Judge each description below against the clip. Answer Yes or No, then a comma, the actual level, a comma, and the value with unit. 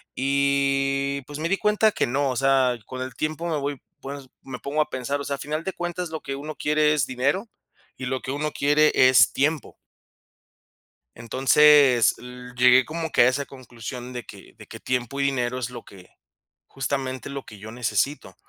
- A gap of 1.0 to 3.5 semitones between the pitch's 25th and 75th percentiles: Yes, average, 2.8 semitones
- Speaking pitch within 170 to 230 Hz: No, low, 135 Hz